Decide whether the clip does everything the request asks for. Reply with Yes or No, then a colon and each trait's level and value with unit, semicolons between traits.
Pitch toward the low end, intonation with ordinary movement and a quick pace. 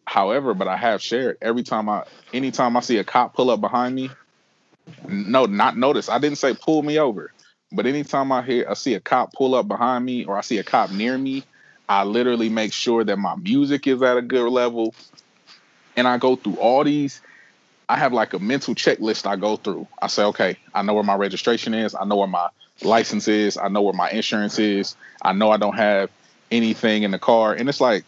Yes: low, 120 Hz; average, 3.7 semitones; fast, 225 wpm